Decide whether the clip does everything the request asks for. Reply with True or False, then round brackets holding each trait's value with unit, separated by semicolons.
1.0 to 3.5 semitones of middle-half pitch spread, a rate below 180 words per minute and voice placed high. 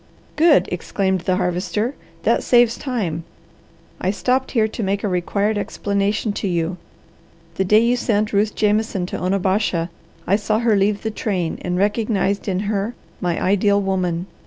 True (2.7 semitones; 160 wpm; 200 Hz)